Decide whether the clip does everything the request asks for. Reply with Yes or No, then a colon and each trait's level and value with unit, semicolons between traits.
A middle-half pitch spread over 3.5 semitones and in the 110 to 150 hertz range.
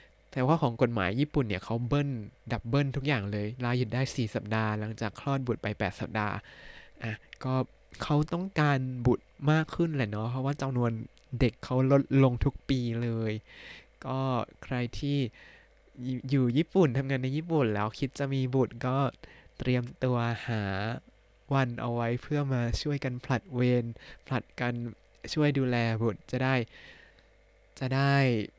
No: average, 3.1 semitones; low, 125 Hz